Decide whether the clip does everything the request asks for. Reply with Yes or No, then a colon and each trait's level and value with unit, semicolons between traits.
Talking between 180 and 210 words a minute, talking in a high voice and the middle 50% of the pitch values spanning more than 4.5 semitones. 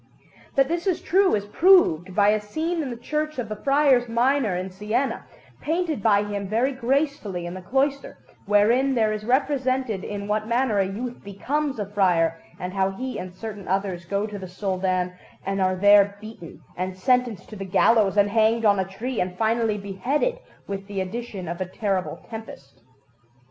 Yes: average, 185 wpm; high, 210 Hz; average, 5.0 semitones